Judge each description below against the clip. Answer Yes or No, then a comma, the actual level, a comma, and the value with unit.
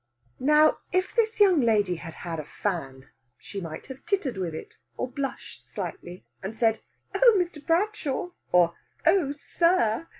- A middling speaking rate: Yes, average, 155 wpm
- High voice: Yes, very high, 265 Hz